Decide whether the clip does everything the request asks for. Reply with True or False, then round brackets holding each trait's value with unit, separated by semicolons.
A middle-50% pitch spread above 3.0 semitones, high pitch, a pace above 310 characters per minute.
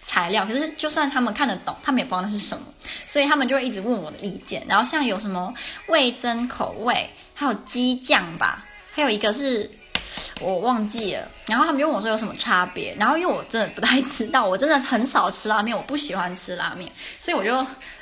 True (5.2 semitones; 250 Hz; 335 characters per minute)